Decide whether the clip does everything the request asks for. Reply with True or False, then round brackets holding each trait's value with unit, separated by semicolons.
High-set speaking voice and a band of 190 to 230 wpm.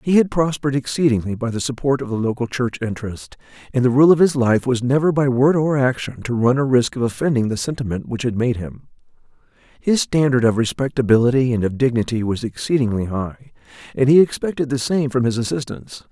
False (130 Hz; 200 wpm)